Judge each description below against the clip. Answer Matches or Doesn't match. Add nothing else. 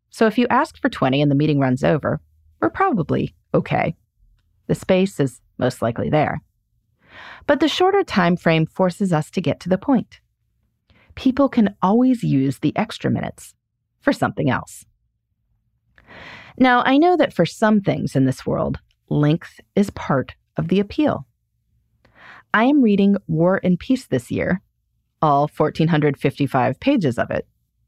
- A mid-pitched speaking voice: Matches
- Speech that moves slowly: Doesn't match